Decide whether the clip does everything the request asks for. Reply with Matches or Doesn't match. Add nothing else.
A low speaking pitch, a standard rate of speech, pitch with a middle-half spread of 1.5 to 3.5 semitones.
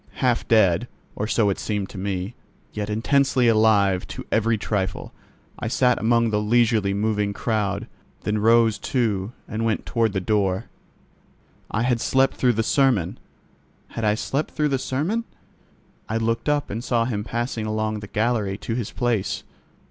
Matches